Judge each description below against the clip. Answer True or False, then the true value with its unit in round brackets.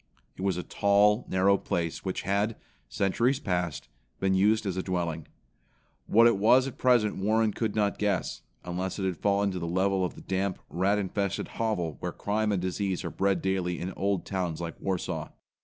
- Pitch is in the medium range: False (95 Hz)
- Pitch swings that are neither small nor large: False (2.2 semitones)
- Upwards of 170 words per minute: True (190 wpm)